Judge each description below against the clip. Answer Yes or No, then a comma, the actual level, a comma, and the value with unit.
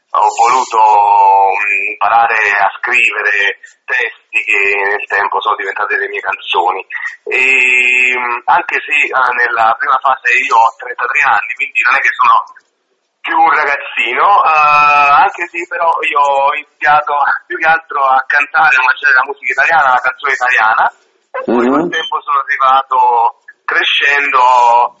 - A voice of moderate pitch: Yes, medium, 160 Hz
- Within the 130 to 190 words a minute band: Yes, average, 135 wpm